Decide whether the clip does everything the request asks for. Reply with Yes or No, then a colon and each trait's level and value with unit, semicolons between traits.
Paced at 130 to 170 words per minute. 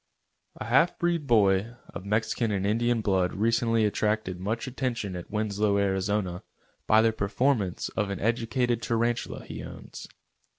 Yes: average, 140 wpm